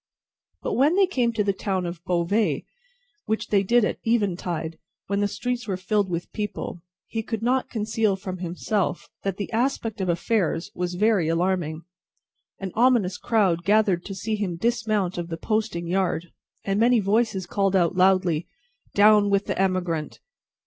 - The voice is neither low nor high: No, high, 195 Hz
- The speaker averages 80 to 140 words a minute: No, average, 165 wpm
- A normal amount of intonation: Yes, average, 3.6 semitones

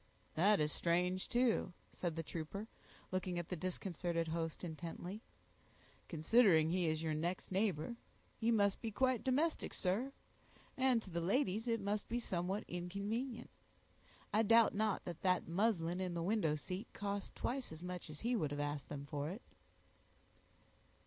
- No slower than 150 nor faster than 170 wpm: Yes, average, 160 wpm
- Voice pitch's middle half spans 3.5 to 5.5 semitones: Yes, average, 4.9 semitones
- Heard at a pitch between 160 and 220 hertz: Yes, medium, 185 Hz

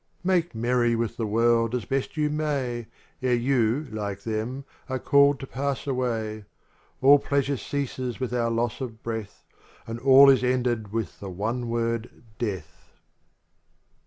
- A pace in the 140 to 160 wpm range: Yes, average, 150 wpm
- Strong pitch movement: No, average, 3.0 semitones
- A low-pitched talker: Yes, low, 120 Hz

